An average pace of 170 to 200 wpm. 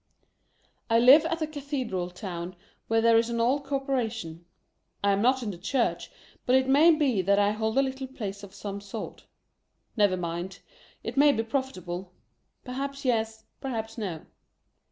Yes: average, 175 wpm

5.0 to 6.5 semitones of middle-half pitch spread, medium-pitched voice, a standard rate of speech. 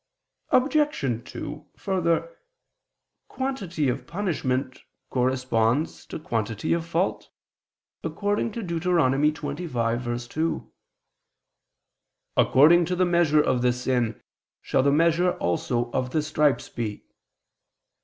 No: wide, 5.5 semitones; medium, 150 Hz; slow, 100 wpm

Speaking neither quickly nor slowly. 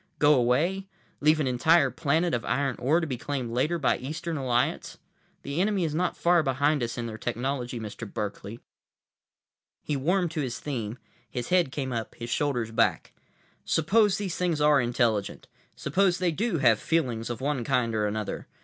Yes: average, 175 wpm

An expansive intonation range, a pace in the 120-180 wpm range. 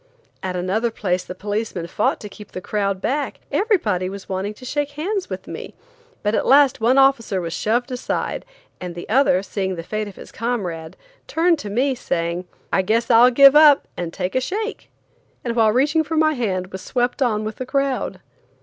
No: wide, 6.4 semitones; average, 195 wpm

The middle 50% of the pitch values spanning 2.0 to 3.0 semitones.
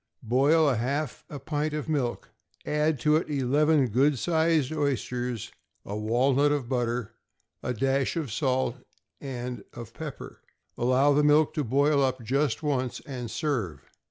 No: average, 3.4 semitones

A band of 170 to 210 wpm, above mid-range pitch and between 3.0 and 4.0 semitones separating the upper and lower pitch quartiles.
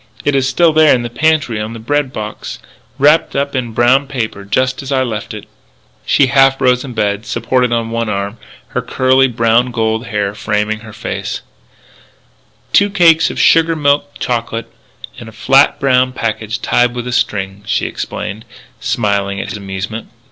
No: average, 180 wpm; low, 120 Hz; average, 3.7 semitones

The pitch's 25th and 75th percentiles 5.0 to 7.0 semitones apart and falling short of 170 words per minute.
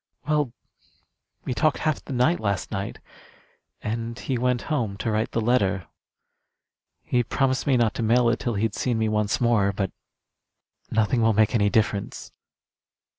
No: average, 2.8 semitones; average, 160 wpm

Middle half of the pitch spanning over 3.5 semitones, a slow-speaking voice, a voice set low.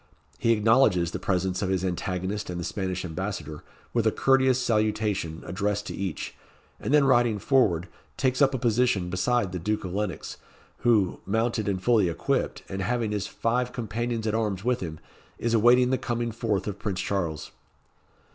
No: average, 4.3 semitones; average, 175 wpm; low, 105 Hz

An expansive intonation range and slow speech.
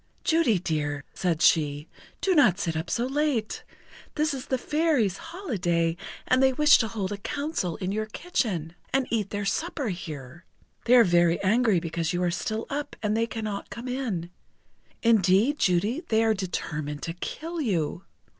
No: wide, 7.0 semitones; average, 170 wpm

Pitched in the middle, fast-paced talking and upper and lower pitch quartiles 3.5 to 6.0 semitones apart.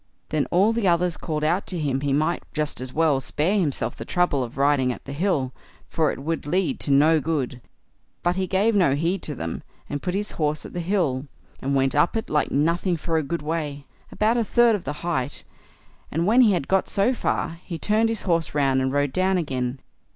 Yes: medium, 160 Hz; fast, 225 wpm; average, 4.7 semitones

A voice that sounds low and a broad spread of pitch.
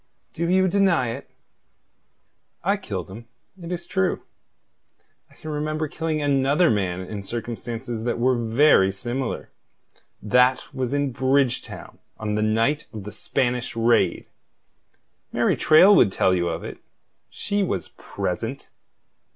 Yes: low, 125 Hz; wide, 5.7 semitones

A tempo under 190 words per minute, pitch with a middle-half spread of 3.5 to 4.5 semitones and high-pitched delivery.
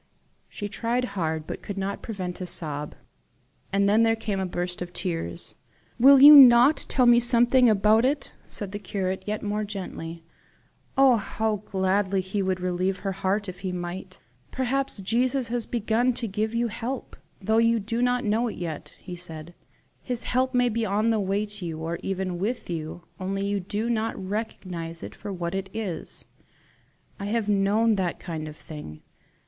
Yes: average, 180 wpm; average, 4.0 semitones; high, 205 Hz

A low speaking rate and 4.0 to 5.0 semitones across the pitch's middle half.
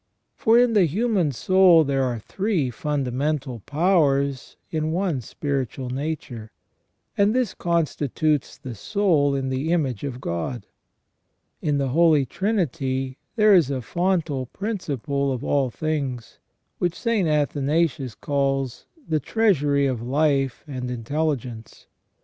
Yes: slow, 130 wpm; average, 4.5 semitones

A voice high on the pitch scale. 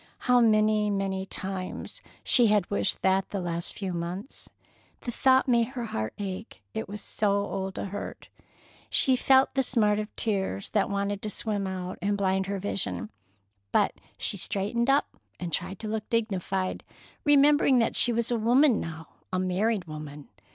Yes: high, 205 Hz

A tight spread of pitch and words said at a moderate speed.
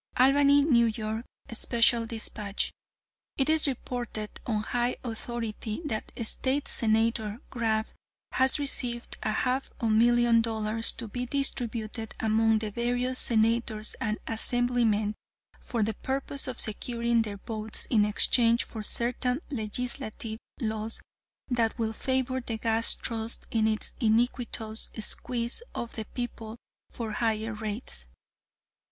No: narrow, 2.1 semitones; slow, 120 wpm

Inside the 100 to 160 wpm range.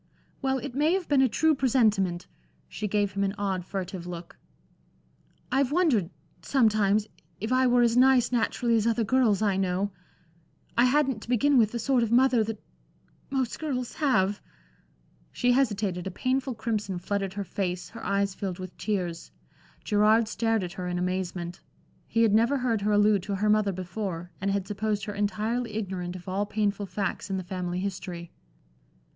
No: average, 175 wpm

